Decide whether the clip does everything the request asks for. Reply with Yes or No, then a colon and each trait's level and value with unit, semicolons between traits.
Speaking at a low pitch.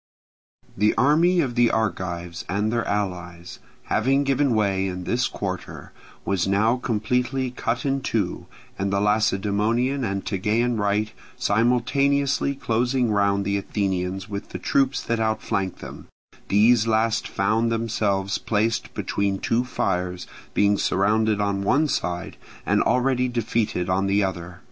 Yes: low, 110 Hz